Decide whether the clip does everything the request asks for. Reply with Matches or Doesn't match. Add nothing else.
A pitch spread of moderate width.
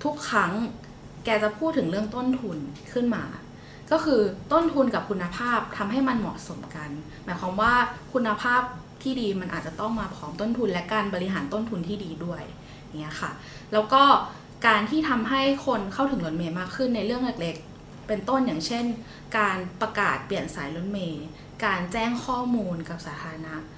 Doesn't match